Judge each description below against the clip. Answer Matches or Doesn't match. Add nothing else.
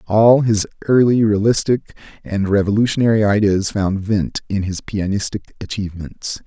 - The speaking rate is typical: Doesn't match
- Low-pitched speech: Matches